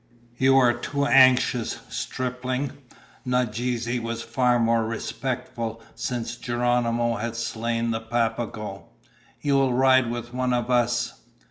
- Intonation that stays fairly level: Yes, narrow, 1.5 semitones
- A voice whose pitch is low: Yes, low, 120 Hz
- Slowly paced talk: Yes, slow, 120 wpm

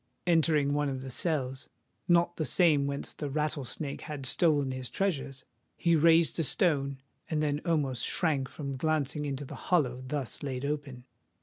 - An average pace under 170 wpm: Yes, average, 150 wpm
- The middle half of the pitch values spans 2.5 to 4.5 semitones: Yes, average, 2.9 semitones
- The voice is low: No, medium, 145 Hz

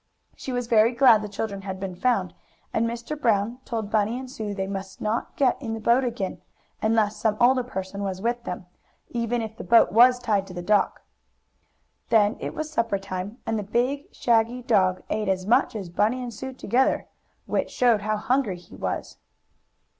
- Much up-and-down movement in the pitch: No, average, 3.4 semitones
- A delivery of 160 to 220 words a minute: Yes, average, 190 wpm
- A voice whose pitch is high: Yes, high, 225 Hz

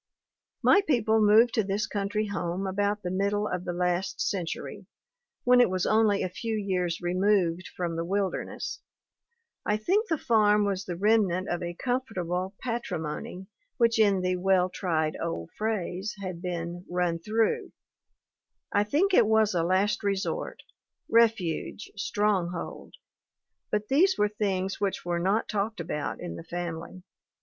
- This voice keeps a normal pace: Yes, average, 150 wpm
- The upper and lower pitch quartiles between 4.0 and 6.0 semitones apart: No, average, 3.2 semitones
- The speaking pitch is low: No, high, 195 Hz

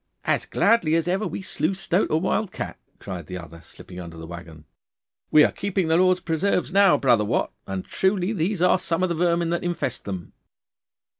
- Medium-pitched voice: Yes, medium, 170 Hz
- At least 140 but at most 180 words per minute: No, average, 200 wpm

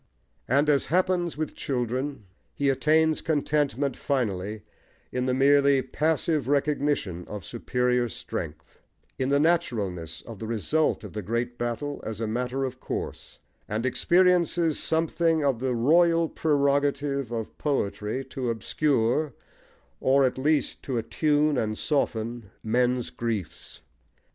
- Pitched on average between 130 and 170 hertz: Yes, low, 135 Hz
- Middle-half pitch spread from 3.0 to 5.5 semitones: Yes, average, 4.3 semitones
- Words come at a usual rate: No, slow, 130 wpm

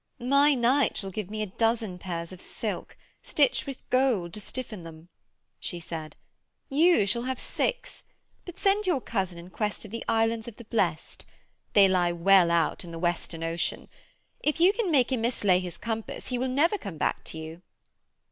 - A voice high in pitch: Yes, high, 215 Hz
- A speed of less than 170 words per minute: No, average, 185 wpm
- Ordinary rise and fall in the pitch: No, wide, 6.7 semitones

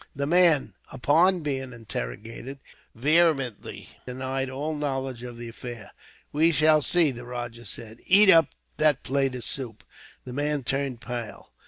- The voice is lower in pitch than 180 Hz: Yes, low, 135 Hz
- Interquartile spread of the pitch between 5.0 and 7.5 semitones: No, average, 3.8 semitones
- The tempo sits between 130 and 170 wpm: Yes, average, 145 wpm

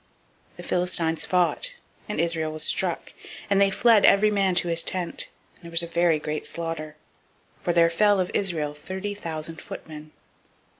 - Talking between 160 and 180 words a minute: Yes, average, 170 wpm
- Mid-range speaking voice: Yes, medium, 170 Hz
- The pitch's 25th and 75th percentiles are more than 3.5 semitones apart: No, average, 3.1 semitones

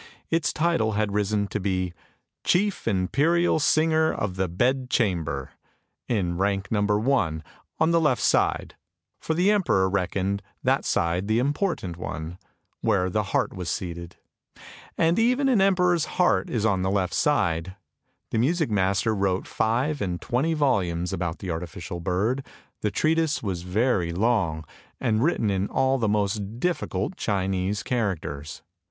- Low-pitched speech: Yes, low, 105 Hz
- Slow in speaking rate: No, average, 150 wpm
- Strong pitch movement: Yes, wide, 7.5 semitones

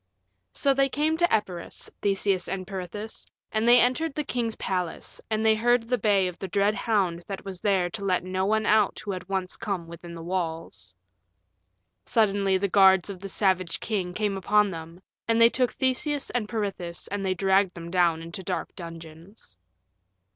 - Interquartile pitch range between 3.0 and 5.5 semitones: Yes, average, 3.3 semitones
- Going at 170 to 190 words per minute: Yes, average, 185 wpm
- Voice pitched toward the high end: Yes, high, 195 Hz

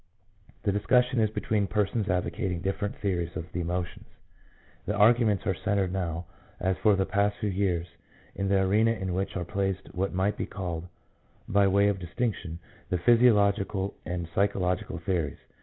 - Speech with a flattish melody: Yes, narrow, 2.3 semitones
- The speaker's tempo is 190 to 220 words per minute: No, average, 165 wpm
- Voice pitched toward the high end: No, very low, 95 Hz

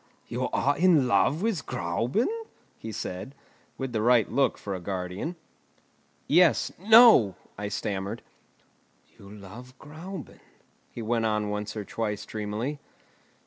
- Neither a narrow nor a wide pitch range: No, wide, 5.9 semitones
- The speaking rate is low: Yes, slow, 130 wpm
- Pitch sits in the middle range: No, low, 115 Hz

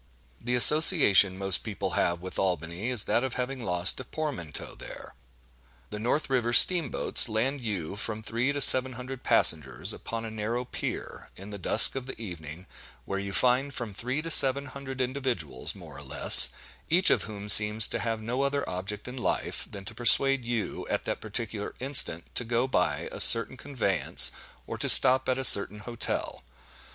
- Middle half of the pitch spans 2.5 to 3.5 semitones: No, average, 4.8 semitones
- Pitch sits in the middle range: No, low, 115 Hz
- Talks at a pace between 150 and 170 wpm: No, average, 185 wpm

